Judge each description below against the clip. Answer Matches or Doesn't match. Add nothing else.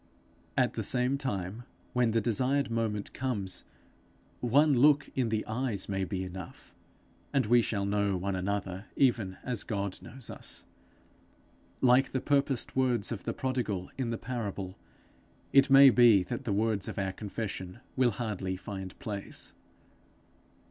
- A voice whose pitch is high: Doesn't match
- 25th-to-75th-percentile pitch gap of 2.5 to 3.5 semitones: Doesn't match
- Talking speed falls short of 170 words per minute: Matches